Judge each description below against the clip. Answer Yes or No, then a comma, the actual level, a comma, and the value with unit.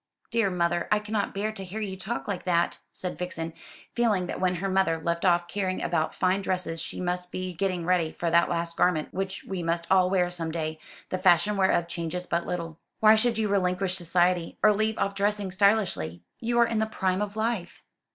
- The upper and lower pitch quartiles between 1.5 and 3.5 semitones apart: Yes, average, 2.8 semitones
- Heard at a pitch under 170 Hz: No, medium, 185 Hz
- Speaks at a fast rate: Yes, fast, 210 wpm